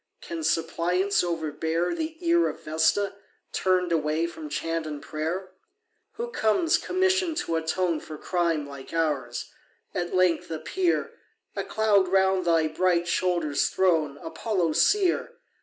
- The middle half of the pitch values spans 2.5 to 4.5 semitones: Yes, average, 3.9 semitones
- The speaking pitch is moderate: Yes, medium, 175 Hz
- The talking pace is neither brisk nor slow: No, slow, 130 wpm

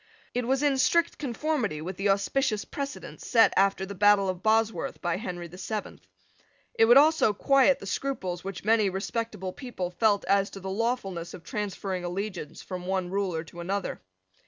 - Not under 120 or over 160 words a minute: No, average, 175 wpm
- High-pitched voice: Yes, high, 200 Hz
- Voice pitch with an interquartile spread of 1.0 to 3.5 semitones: No, average, 3.9 semitones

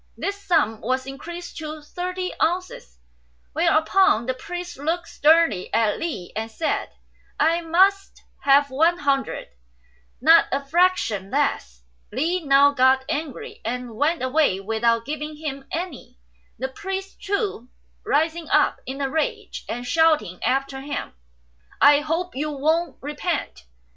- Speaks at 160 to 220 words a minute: No, slow, 135 wpm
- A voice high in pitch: Yes, very high, 295 Hz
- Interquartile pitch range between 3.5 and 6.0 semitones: Yes, average, 4.5 semitones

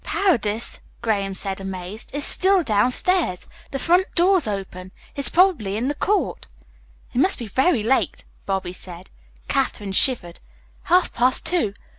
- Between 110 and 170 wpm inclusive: Yes, average, 140 wpm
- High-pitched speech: Yes, high, 235 Hz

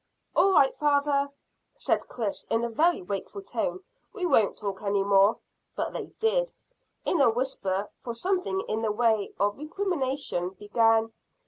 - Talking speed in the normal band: Yes, average, 150 wpm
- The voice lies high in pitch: Yes, high, 235 Hz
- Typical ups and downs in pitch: No, wide, 7.8 semitones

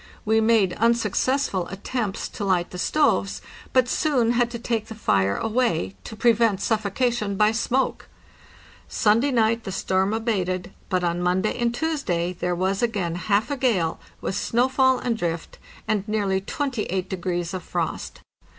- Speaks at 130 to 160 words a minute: Yes, average, 150 wpm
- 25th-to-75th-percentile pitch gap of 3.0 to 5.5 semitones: Yes, average, 4.2 semitones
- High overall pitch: Yes, high, 215 Hz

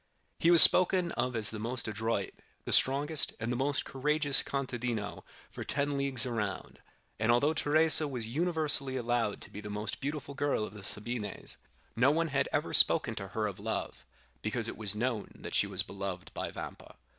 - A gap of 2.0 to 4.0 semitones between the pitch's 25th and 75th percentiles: No, average, 5.1 semitones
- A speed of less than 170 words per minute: No, average, 185 wpm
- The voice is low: Yes, low, 125 Hz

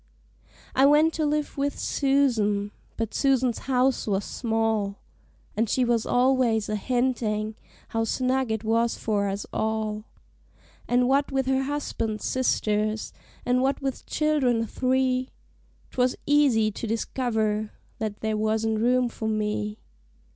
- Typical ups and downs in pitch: Yes, average, 3.3 semitones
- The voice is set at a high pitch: Yes, high, 235 Hz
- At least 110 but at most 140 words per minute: Yes, slow, 135 wpm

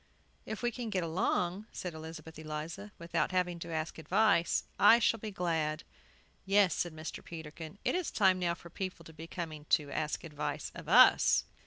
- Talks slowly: No, average, 180 wpm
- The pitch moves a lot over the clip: No, average, 3.4 semitones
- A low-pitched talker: No, medium, 170 Hz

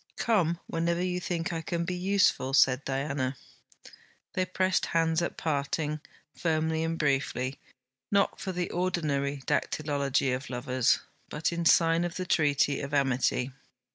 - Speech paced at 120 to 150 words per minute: Yes, average, 140 wpm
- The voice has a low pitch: No, medium, 160 Hz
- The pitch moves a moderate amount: Yes, average, 3.8 semitones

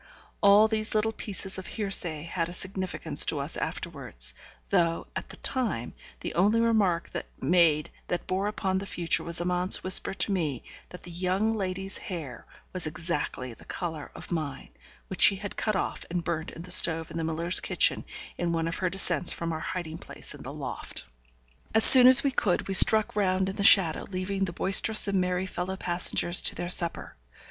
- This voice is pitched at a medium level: Yes, medium, 180 Hz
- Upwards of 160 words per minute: Yes, average, 190 wpm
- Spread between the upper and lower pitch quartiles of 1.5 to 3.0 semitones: Yes, average, 2.7 semitones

